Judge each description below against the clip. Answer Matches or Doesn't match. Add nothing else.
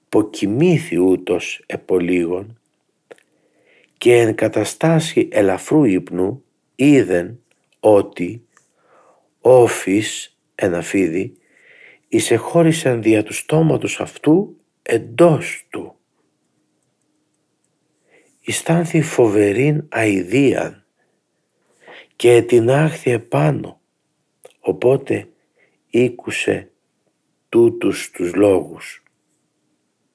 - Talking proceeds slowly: Matches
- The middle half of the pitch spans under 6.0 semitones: Doesn't match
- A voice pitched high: Doesn't match